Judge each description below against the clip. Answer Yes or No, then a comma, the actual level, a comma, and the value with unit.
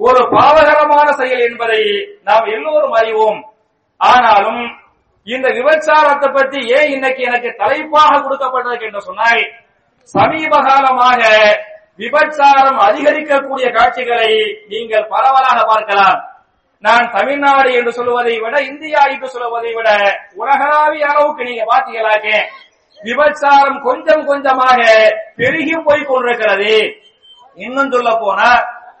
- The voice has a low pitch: No, very high, 255 Hz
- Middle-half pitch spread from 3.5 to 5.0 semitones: Yes, average, 4.4 semitones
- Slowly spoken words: Yes, slow, 85 wpm